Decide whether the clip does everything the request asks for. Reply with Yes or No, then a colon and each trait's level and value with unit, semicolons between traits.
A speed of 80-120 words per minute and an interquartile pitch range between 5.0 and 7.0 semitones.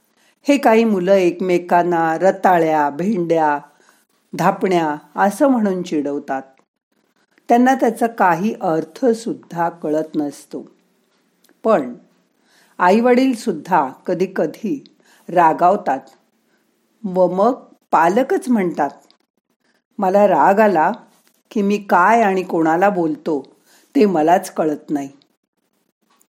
Yes: average, 85 wpm; wide, 5.5 semitones